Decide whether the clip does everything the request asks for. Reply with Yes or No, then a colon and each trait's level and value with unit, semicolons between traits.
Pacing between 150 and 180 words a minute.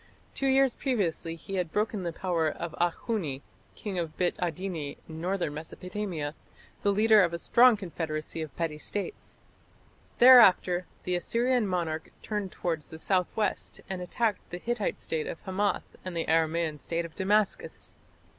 Yes: average, 155 wpm